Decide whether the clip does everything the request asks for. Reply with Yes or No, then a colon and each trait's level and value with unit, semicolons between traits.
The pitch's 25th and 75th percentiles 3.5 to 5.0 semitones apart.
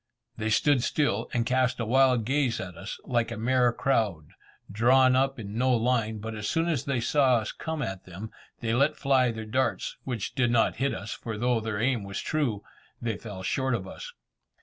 No: average, 3.1 semitones